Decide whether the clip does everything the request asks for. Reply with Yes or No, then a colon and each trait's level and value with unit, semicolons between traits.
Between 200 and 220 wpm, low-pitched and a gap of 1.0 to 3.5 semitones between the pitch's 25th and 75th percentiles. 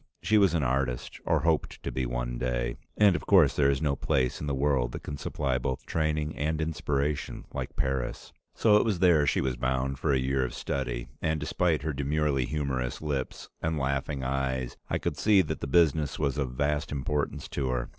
Yes: fast, 205 wpm; very low, 70 Hz; average, 2.9 semitones